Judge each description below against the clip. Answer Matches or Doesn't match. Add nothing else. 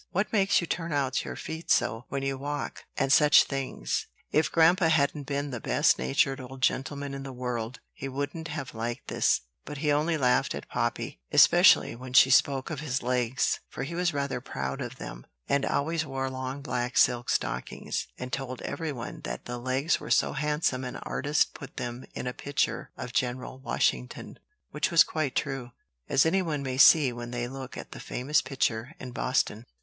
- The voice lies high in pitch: Doesn't match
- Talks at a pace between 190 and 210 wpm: Matches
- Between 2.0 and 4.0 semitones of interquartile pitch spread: Matches